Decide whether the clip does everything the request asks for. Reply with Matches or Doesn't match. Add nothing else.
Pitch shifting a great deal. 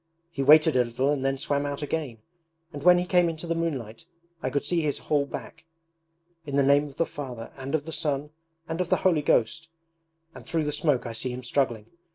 Doesn't match